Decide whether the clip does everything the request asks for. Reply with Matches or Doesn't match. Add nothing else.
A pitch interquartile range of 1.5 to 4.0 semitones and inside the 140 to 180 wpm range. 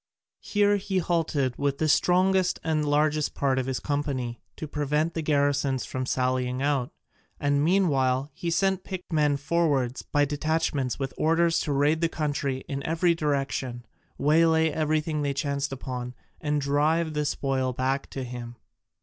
Matches